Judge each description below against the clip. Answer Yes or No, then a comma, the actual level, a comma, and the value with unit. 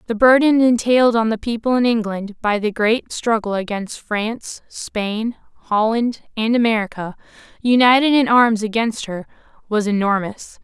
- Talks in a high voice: Yes, high, 225 Hz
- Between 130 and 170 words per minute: Yes, average, 140 wpm